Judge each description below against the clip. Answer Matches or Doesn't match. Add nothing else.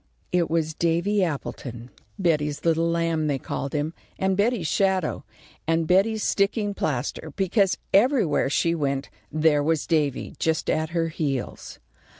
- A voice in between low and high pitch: Matches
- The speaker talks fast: Doesn't match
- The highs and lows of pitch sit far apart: Doesn't match